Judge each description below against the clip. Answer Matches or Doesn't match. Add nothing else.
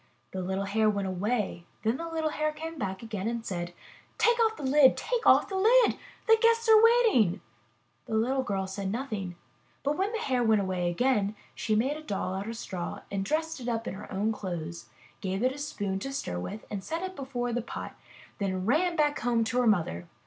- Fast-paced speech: Matches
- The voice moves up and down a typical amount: Doesn't match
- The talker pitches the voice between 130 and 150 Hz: Doesn't match